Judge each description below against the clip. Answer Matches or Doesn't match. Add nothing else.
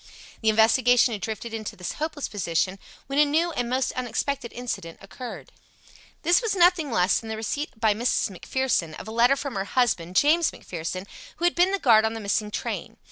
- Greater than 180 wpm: Matches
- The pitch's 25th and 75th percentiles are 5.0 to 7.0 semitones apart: Matches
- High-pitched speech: Matches